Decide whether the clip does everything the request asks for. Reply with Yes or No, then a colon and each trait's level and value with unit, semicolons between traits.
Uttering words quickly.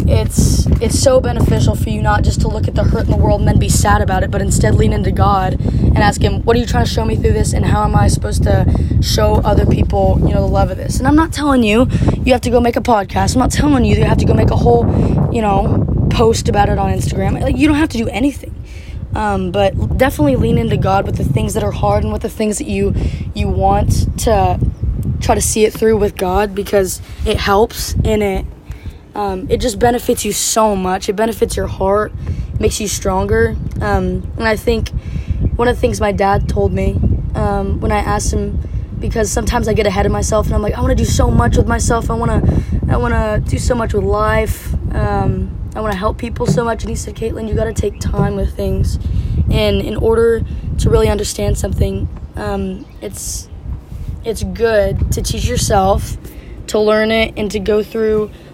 Yes: fast, 230 wpm